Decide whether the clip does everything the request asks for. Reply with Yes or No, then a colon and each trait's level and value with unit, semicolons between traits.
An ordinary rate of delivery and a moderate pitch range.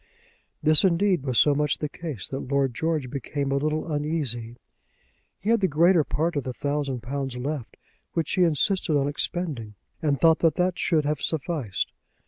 Yes: average, 175 wpm; average, 3.3 semitones